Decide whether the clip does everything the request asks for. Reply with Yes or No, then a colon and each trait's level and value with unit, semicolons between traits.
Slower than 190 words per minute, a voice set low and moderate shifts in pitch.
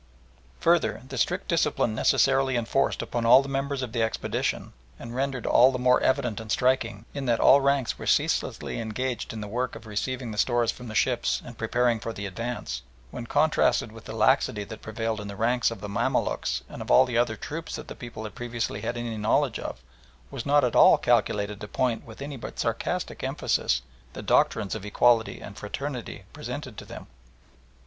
No: average, 195 wpm; low, 120 Hz; average, 3.1 semitones